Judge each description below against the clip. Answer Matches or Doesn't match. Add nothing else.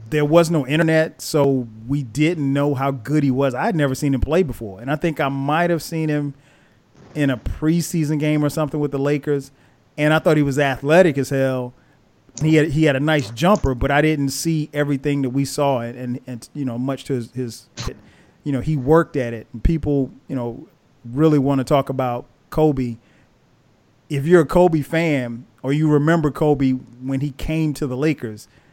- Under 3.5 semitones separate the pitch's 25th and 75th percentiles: Matches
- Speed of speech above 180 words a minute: Matches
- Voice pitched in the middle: Matches